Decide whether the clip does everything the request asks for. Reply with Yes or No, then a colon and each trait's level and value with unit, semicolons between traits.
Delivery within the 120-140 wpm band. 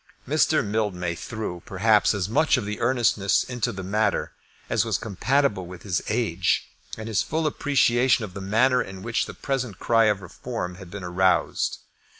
No: average, 165 wpm